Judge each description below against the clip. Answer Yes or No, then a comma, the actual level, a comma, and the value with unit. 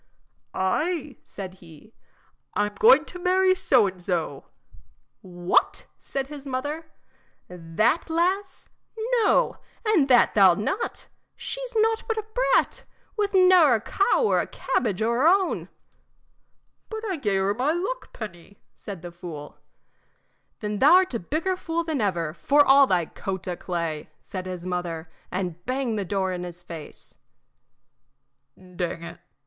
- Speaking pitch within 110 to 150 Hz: No, high, 220 Hz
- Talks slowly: No, average, 150 wpm